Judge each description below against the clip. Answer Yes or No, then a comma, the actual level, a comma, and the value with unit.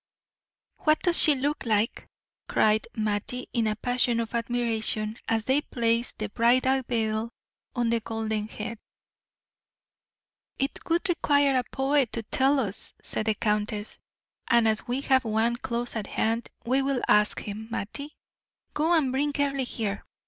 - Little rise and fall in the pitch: No, average, 3.6 semitones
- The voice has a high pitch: Yes, high, 235 Hz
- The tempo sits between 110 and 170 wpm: Yes, average, 150 wpm